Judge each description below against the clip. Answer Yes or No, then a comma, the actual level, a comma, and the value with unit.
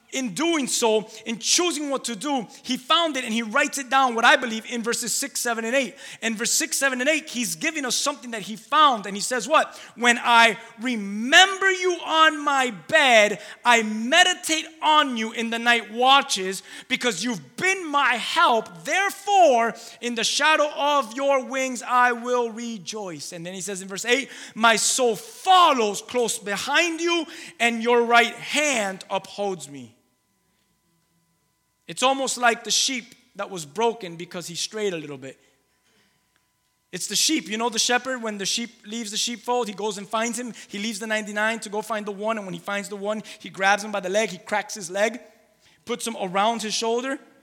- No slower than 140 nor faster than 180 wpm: No, average, 195 wpm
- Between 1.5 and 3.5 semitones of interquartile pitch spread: No, average, 4.4 semitones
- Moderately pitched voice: No, high, 235 Hz